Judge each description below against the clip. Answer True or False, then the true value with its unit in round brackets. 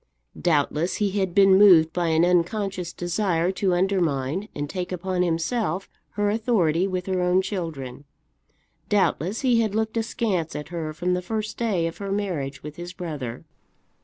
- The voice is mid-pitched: True (180 Hz)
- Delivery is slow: False (160 wpm)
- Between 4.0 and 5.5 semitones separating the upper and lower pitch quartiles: False (3.4 semitones)